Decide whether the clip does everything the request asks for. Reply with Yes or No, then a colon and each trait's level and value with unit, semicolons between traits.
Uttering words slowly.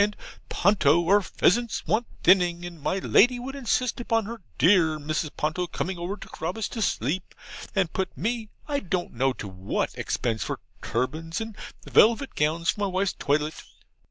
No: average, 170 wpm